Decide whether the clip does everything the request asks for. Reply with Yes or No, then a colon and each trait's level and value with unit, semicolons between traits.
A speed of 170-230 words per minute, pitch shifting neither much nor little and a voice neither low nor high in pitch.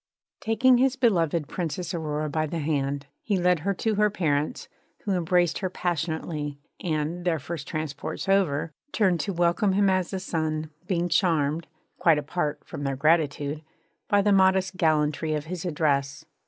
No: average, 160 wpm; average, 3.7 semitones; medium, 165 Hz